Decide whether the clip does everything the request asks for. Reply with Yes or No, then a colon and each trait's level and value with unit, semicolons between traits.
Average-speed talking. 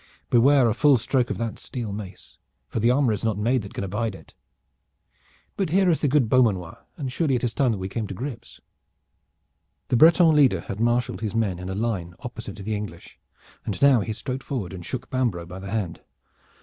No: fast, 215 wpm